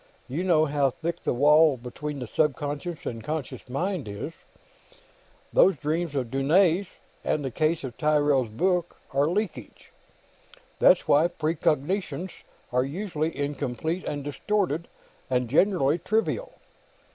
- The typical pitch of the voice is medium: Yes, medium, 150 Hz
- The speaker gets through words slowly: Yes, slow, 130 wpm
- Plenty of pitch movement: No, average, 4.0 semitones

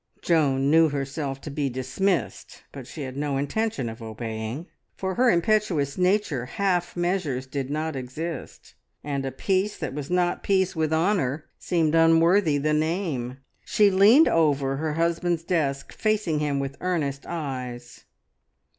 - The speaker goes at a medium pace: Yes, average, 145 wpm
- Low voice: No, medium, 155 Hz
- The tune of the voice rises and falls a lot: No, average, 4.6 semitones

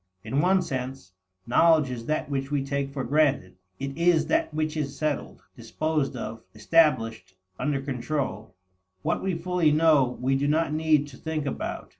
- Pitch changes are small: No, average, 3.2 semitones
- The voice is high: No, medium, 145 Hz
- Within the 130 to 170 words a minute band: Yes, average, 165 wpm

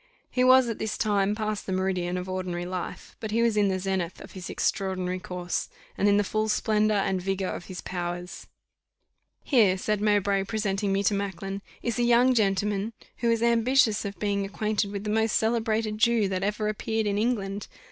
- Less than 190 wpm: No, average, 195 wpm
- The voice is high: Yes, high, 205 Hz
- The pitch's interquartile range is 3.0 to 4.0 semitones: No, narrow, 2.4 semitones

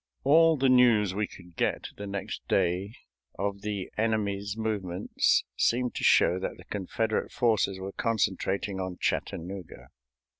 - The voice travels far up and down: No, average, 2.8 semitones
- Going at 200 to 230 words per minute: No, average, 140 wpm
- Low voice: Yes, low, 100 Hz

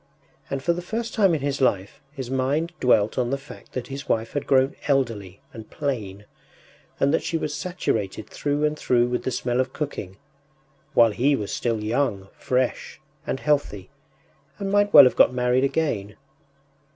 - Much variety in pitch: No, average, 4.4 semitones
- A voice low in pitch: Yes, low, 130 Hz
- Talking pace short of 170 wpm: No, average, 180 wpm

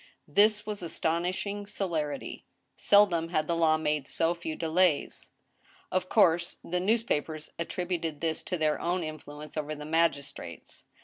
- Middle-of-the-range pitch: Yes, medium, 165 Hz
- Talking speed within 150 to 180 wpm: No, slow, 135 wpm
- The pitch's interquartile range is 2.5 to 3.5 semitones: Yes, average, 2.9 semitones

